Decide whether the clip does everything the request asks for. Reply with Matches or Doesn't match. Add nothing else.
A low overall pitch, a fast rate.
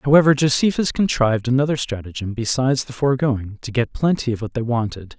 Doesn't match